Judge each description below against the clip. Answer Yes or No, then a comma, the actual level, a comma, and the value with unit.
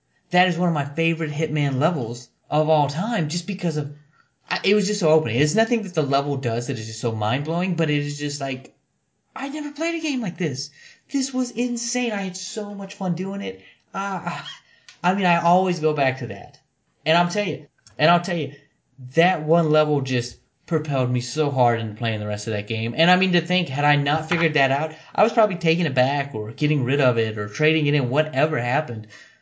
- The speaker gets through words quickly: Yes, fast, 230 wpm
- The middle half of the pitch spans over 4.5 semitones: Yes, average, 4.9 semitones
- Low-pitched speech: No, medium, 155 Hz